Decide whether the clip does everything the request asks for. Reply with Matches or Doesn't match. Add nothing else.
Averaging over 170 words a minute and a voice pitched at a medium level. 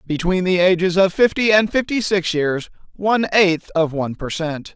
Matches